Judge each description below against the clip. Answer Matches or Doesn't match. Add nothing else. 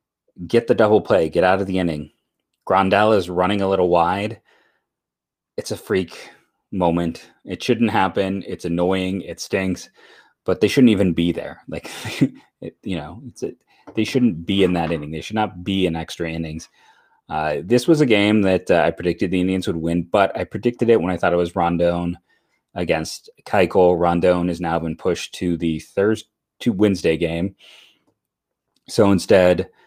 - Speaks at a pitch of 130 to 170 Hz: Doesn't match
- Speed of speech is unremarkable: Matches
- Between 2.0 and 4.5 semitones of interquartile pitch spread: Matches